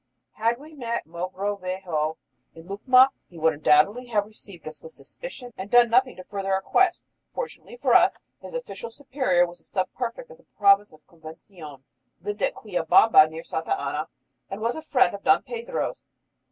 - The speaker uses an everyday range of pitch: No, wide, 6.8 semitones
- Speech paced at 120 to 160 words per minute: No, average, 180 wpm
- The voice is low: No, high, 205 Hz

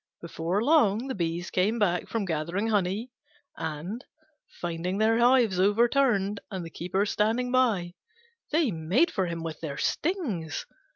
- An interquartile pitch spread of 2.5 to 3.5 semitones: No, wide, 5.5 semitones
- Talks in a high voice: Yes, high, 200 Hz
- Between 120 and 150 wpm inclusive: Yes, average, 140 wpm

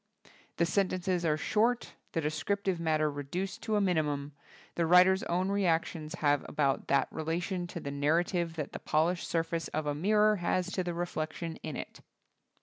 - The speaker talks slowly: No, average, 170 wpm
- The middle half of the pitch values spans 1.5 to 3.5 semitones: Yes, average, 3.2 semitones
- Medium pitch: Yes, medium, 170 Hz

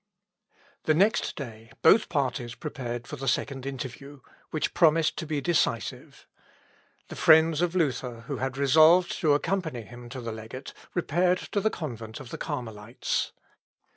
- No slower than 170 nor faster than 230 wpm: No, average, 150 wpm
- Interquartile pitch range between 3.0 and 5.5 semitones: Yes, average, 4.8 semitones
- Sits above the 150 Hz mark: No, medium, 140 Hz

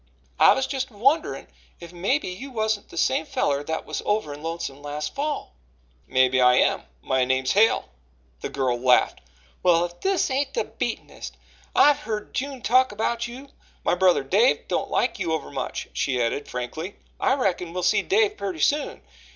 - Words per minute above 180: No, average, 175 wpm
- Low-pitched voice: No, medium, 185 Hz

